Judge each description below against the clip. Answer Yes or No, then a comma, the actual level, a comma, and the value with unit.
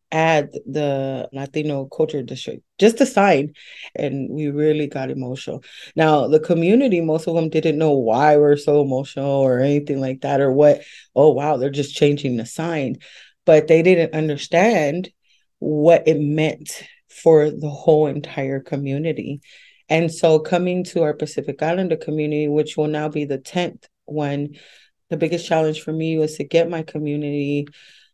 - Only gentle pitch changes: Yes, narrow, 2.1 semitones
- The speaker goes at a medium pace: Yes, average, 160 wpm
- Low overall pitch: No, medium, 150 Hz